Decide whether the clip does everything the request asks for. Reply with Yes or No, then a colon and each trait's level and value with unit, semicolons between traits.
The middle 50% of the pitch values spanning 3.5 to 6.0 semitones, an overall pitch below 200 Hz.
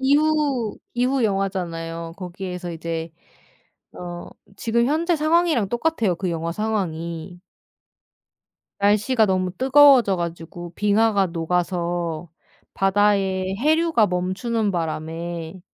Yes: wide, 5.5 semitones; high, 190 Hz